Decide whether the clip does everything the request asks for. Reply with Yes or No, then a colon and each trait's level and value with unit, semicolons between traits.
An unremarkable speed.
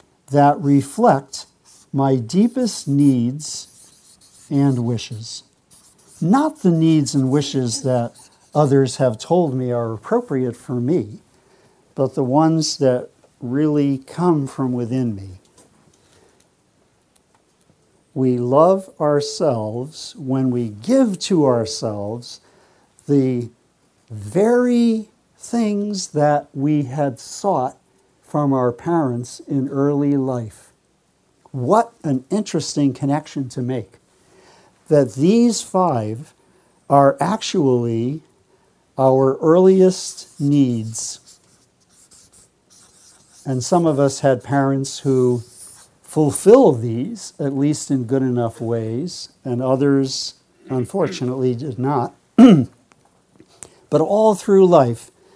No: slow, 95 wpm